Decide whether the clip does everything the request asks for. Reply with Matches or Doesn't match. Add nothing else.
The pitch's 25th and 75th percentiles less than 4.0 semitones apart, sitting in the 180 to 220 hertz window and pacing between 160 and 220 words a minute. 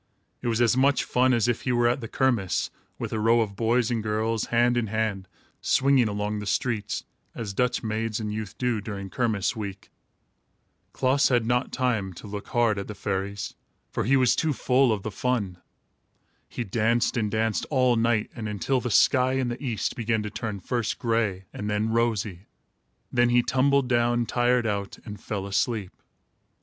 Doesn't match